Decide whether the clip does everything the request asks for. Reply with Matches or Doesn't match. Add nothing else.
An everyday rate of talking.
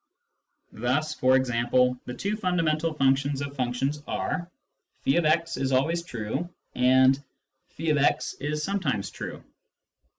Doesn't match